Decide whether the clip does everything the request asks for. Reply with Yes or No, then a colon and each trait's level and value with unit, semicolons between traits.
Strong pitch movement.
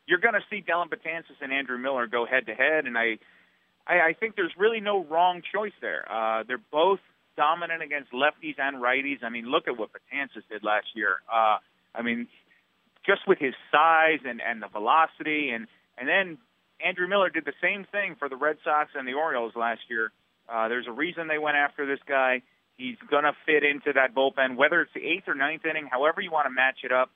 No: average, 4.7 semitones